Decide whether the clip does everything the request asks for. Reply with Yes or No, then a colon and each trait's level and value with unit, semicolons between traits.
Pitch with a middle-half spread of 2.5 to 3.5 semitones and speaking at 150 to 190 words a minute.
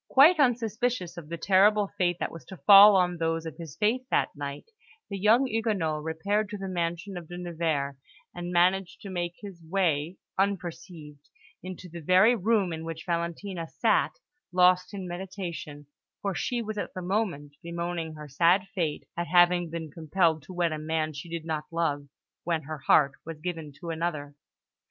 Yes: average, 3.2 semitones; average, 180 wpm